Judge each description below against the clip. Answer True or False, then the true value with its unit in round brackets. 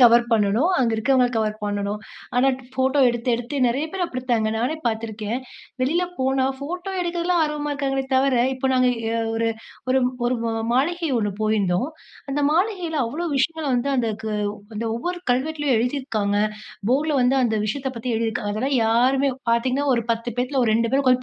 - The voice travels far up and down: False (3.7 semitones)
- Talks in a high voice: True (255 Hz)